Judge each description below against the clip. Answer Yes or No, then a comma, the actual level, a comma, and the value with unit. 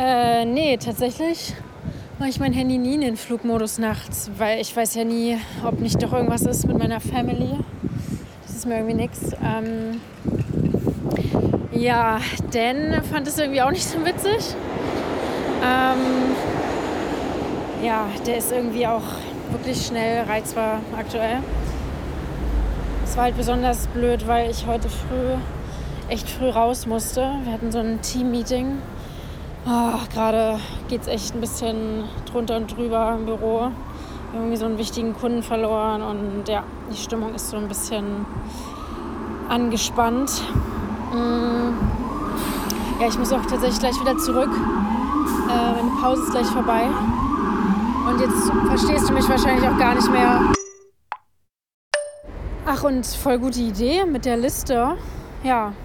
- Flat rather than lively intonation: Yes, narrow, 2.2 semitones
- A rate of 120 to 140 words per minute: Yes, average, 135 wpm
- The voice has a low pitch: No, high, 235 Hz